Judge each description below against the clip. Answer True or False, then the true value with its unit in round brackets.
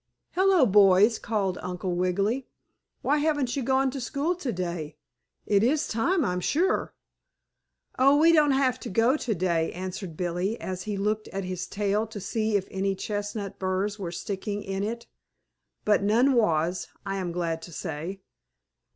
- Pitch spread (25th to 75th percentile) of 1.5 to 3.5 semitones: False (5.1 semitones)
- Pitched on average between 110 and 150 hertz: False (205 Hz)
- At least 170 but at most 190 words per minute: False (160 wpm)